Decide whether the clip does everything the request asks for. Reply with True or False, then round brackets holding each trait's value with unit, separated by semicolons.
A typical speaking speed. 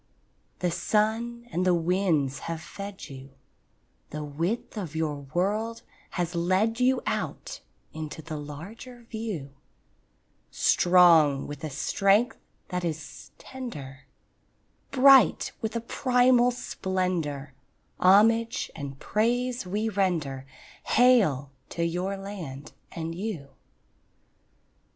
False (105 wpm)